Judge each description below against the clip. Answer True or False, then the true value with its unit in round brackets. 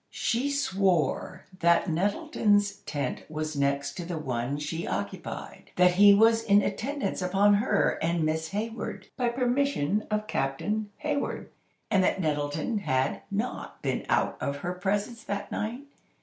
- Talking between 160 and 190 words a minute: False (140 wpm)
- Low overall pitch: False (190 Hz)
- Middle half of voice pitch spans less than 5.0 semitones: False (5.6 semitones)